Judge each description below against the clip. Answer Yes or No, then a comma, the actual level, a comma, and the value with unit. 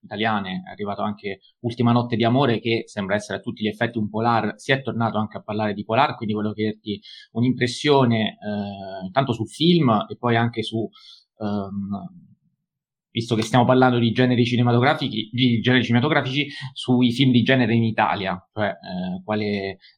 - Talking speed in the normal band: Yes, average, 160 wpm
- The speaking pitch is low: Yes, low, 115 Hz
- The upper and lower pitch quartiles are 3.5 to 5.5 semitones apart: No, average, 3.1 semitones